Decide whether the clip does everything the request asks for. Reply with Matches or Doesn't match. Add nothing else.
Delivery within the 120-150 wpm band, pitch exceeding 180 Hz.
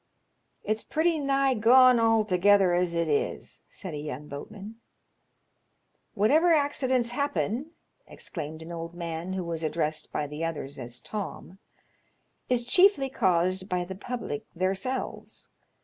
Matches